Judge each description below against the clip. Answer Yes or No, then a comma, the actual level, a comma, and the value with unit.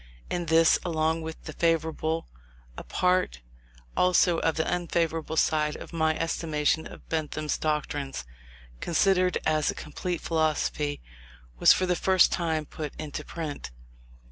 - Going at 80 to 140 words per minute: Yes, slow, 135 wpm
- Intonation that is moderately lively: No, narrow, 1.7 semitones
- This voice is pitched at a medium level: Yes, medium, 160 Hz